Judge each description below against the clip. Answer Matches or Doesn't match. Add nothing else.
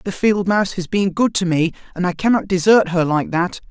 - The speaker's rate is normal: Doesn't match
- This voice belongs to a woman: Doesn't match